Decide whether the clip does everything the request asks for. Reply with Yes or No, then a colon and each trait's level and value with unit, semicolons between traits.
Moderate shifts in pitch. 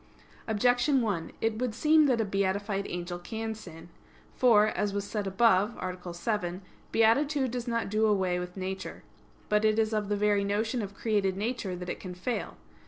Yes: average, 3.1 semitones